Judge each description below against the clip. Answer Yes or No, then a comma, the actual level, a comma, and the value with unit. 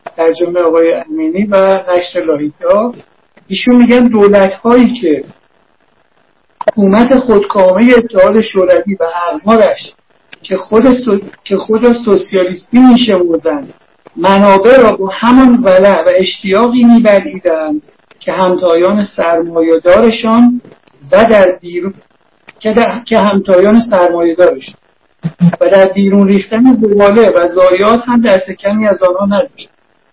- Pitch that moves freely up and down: No, average, 4.1 semitones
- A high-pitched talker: Yes, high, 195 Hz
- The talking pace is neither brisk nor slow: Yes, average, 115 wpm